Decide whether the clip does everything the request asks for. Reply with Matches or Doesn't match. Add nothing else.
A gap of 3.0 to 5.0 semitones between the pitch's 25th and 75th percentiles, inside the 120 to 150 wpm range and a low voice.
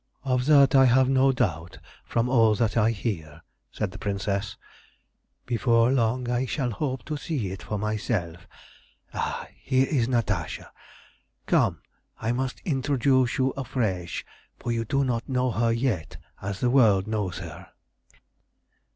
Matches